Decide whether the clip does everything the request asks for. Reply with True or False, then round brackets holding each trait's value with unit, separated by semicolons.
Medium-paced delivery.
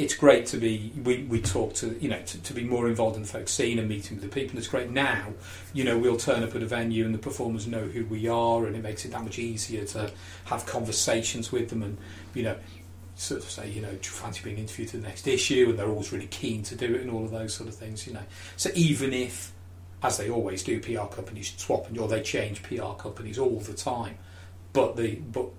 False (255 wpm)